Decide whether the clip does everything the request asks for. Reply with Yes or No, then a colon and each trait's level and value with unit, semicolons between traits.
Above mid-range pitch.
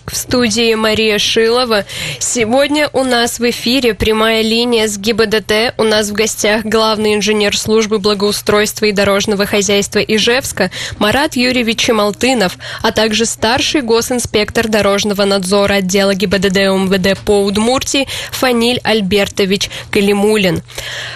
Yes: high, 215 Hz